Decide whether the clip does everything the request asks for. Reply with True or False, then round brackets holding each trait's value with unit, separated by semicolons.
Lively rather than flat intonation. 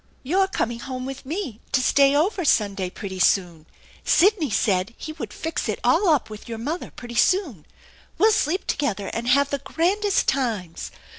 True (7.2 semitones)